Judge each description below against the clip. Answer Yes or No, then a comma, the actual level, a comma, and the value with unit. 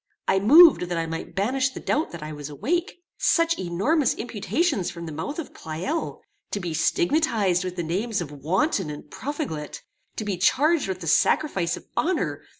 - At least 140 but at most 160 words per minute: No, average, 180 wpm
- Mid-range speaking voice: No, high, 195 Hz